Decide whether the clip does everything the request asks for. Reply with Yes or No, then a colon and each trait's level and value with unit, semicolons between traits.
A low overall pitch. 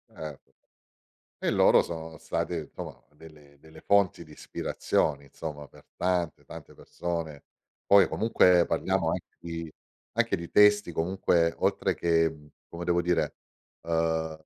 Yes: very low, 85 Hz